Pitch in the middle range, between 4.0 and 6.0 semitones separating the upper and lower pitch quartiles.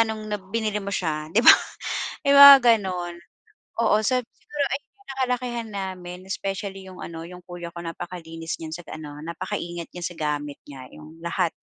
Yes: medium, 180 Hz; average, 4.6 semitones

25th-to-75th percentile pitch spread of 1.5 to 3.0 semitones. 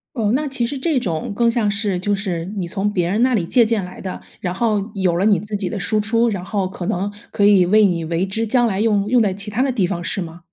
No: average, 3.5 semitones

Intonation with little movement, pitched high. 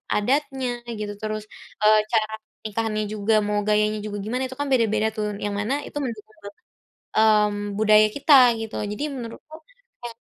Yes: narrow, 1.6 semitones; high, 215 Hz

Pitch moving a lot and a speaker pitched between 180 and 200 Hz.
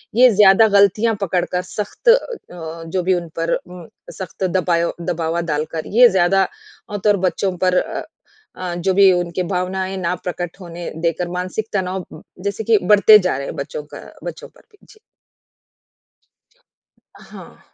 No: narrow, 2.6 semitones; medium, 185 Hz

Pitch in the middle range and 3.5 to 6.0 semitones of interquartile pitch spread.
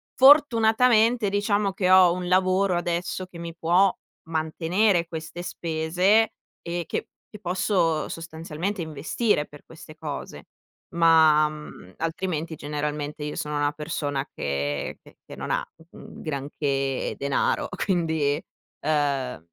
Yes: medium, 165 Hz; average, 3.8 semitones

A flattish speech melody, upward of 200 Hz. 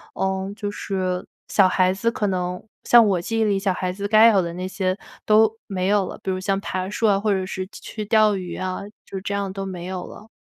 No: narrow, 2.0 semitones; high, 195 Hz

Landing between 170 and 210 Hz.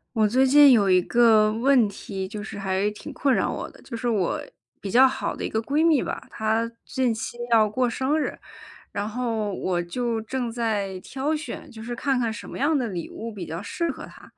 No: high, 230 Hz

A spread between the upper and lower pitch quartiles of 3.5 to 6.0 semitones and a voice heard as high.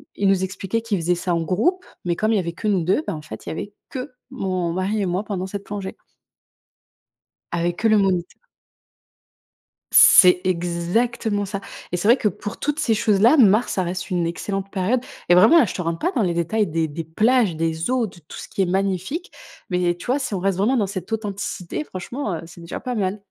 Yes: average, 3.8 semitones; high, 195 Hz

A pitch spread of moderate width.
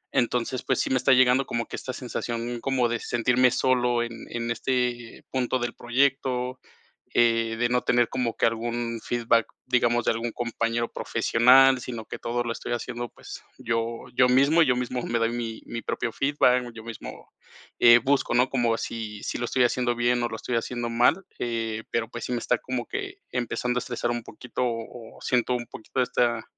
No: narrow, 1.3 semitones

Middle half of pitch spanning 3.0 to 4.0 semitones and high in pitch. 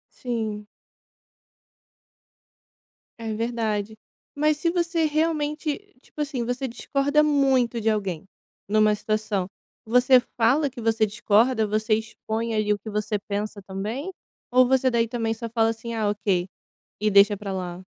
Yes: average, 3.6 semitones; high, 225 Hz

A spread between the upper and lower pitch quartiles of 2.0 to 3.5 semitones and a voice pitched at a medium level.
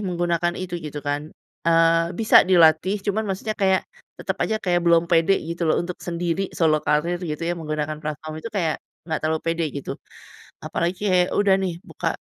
Yes: average, 2.7 semitones; medium, 170 Hz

